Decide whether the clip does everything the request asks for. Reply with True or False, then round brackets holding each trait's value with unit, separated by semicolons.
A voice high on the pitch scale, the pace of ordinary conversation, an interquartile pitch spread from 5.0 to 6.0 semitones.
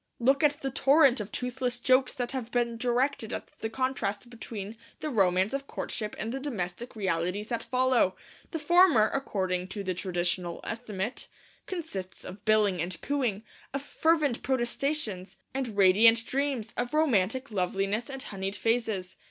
True (230 Hz; 150 wpm; 5.3 semitones)